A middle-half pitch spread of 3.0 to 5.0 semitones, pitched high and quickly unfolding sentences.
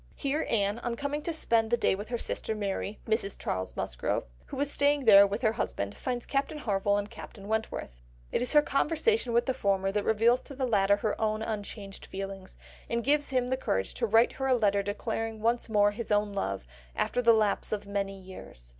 Yes: average, 3.6 semitones; high, 220 Hz; fast, 210 wpm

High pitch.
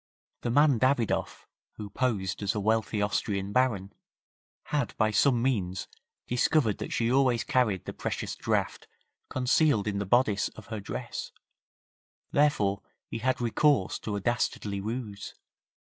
No: low, 110 Hz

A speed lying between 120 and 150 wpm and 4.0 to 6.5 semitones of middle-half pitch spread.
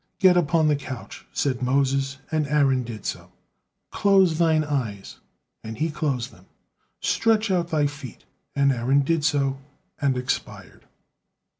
No: average, 140 wpm; average, 3.4 semitones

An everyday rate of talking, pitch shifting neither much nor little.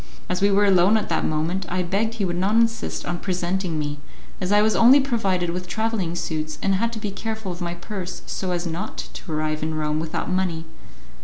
No: fast, 220 wpm; average, 3.3 semitones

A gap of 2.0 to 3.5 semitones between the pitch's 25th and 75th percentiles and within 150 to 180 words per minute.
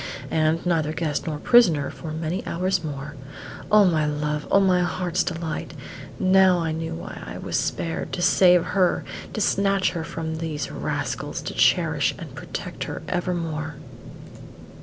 Yes: average, 2.7 semitones; average, 155 wpm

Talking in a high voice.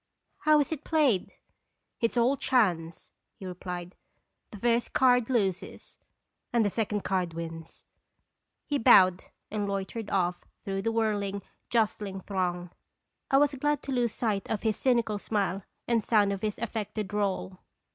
Yes: high, 210 Hz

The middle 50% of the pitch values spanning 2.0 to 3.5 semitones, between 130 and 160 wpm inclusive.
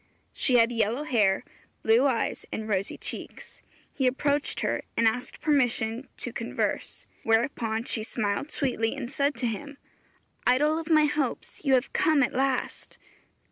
No: average, 4.0 semitones; average, 150 wpm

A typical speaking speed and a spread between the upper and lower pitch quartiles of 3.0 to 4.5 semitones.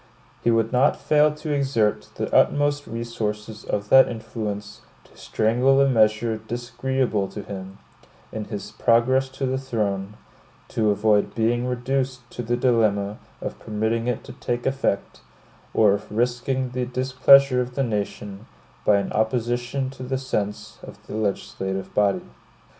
Yes: average, 145 wpm; average, 3.5 semitones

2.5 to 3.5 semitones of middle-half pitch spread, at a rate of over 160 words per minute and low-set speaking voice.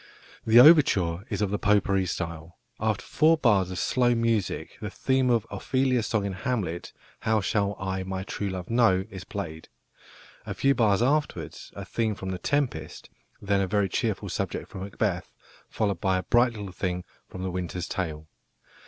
No: average, 3.9 semitones; average, 175 wpm; low, 100 Hz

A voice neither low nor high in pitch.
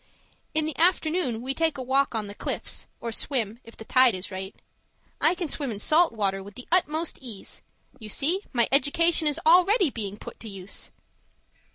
No: very high, 260 Hz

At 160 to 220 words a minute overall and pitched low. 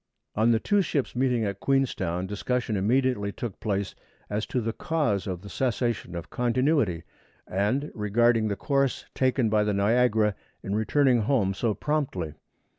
Yes: average, 165 wpm; low, 115 Hz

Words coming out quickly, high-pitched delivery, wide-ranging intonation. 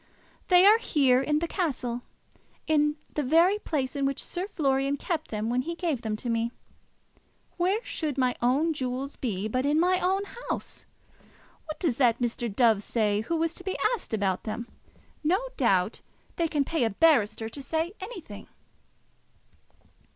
No: average, 165 wpm; very high, 280 Hz; wide, 5.8 semitones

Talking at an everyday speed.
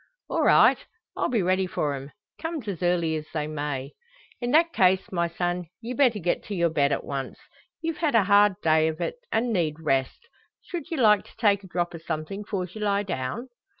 No: fast, 210 wpm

